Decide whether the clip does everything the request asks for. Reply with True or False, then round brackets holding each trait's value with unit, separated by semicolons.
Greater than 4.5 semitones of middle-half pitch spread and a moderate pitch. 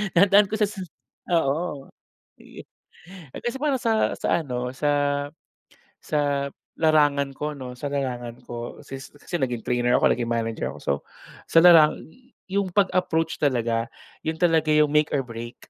True (5.2 semitones; 145 Hz)